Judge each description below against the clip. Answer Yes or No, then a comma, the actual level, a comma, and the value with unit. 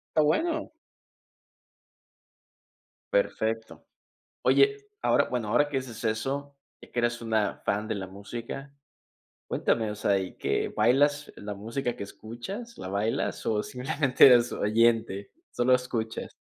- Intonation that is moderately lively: Yes, average, 4.3 semitones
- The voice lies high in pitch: No, low, 120 Hz